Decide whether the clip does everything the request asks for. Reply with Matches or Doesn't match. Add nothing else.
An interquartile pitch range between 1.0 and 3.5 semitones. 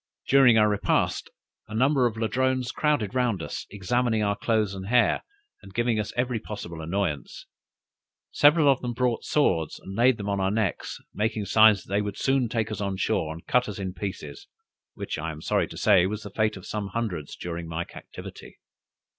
Doesn't match